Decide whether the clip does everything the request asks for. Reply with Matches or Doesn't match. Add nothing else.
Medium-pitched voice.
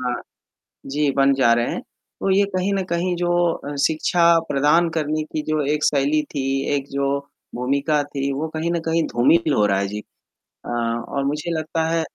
Matches